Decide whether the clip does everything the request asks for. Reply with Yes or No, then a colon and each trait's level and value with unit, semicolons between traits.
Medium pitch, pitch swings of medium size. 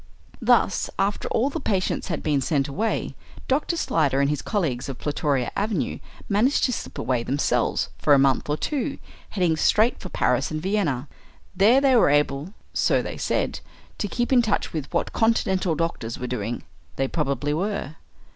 No: medium, 165 Hz; wide, 7.4 semitones